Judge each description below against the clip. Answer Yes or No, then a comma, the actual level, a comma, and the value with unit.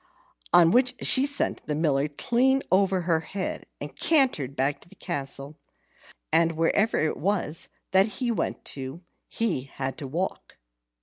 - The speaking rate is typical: Yes, average, 150 wpm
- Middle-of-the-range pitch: Yes, medium, 170 Hz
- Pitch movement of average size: No, wide, 6.8 semitones